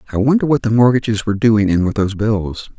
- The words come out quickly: Yes, fast, 235 wpm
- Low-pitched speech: Yes, low, 110 Hz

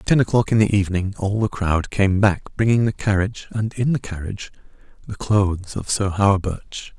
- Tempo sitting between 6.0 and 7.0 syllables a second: No, 5.4 syllables/s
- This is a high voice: No, low, 100 Hz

